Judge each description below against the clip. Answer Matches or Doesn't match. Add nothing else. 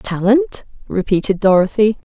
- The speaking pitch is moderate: Doesn't match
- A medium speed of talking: Doesn't match